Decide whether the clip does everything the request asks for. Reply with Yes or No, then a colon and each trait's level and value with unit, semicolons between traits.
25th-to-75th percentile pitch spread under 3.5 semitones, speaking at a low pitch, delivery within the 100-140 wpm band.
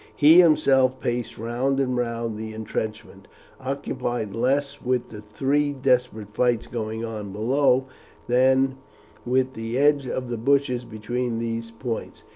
Yes: average, 2.8 semitones; low, 125 Hz; slow, 135 wpm